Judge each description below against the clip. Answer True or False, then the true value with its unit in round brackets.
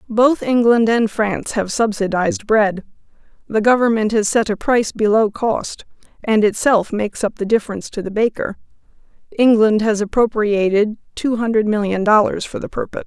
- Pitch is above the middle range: True (215 Hz)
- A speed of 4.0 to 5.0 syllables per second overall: False (5.3 syllables/s)